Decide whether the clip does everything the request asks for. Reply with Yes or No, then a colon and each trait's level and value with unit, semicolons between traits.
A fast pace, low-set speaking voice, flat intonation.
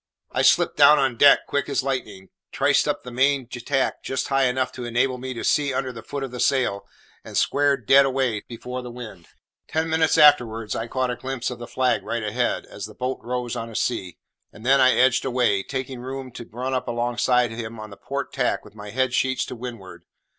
Yes: fast, 220 wpm; low, 125 Hz; narrow, 2.1 semitones